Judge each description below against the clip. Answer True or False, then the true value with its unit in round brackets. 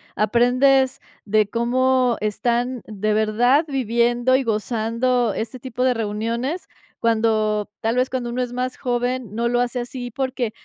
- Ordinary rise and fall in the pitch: False (2.3 semitones)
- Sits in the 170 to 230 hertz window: False (240 Hz)